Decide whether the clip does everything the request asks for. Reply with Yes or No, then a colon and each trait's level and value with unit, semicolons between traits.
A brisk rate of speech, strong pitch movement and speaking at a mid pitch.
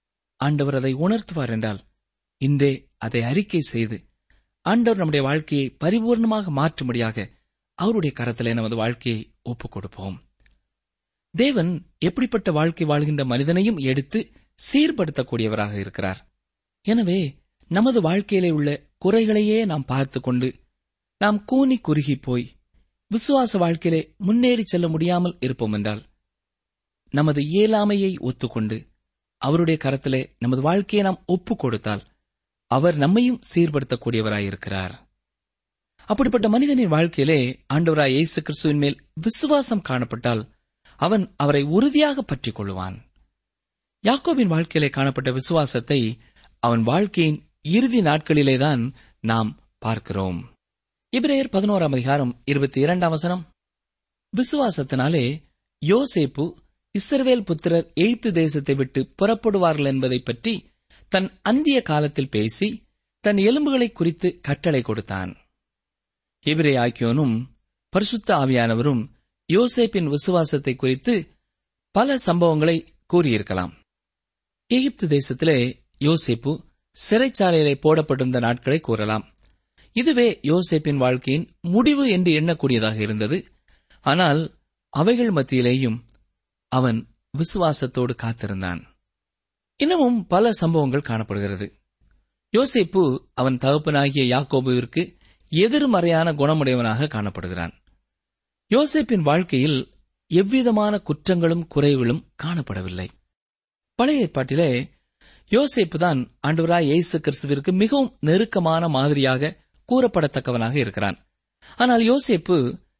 No: average, 90 wpm; wide, 7.8 semitones; medium, 150 Hz